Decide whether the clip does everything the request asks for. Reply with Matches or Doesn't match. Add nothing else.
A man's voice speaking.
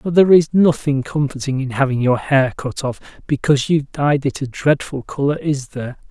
Matches